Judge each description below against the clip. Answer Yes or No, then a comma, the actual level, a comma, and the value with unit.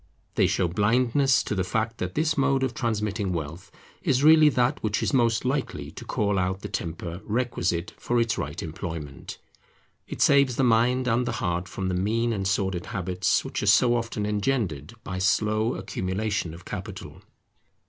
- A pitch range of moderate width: Yes, average, 4.8 semitones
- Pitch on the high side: No, low, 105 Hz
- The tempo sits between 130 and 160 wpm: No, average, 175 wpm